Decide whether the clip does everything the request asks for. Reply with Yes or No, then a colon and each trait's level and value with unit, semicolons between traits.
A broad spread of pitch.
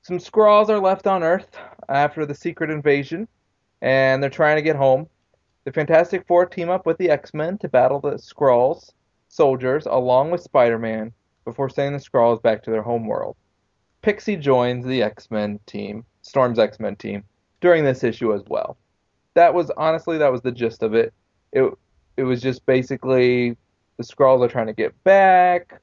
Yes: wide, 6.4 semitones